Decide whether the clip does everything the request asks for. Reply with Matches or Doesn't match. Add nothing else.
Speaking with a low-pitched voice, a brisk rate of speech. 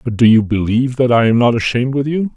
Matches